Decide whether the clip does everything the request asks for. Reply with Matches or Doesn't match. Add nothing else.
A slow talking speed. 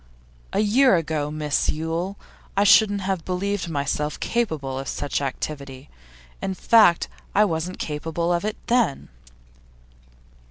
Matches